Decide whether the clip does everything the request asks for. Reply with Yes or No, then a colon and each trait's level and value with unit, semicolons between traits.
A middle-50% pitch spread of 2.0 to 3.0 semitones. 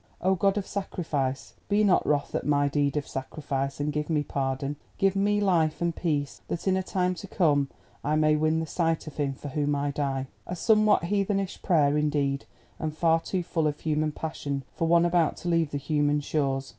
No: average, 3.5 semitones